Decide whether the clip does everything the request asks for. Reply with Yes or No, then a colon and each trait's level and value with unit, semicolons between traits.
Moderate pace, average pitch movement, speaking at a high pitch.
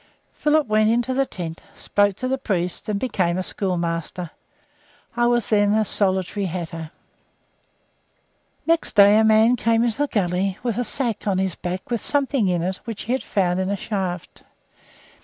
Yes: average, 175 wpm; average, 4.4 semitones; high, 205 Hz